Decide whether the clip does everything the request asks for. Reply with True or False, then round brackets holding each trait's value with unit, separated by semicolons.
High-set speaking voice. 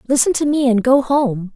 True (255 Hz)